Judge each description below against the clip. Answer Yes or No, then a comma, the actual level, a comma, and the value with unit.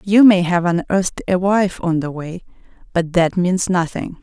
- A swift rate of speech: No, average, 185 wpm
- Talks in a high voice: No, medium, 180 Hz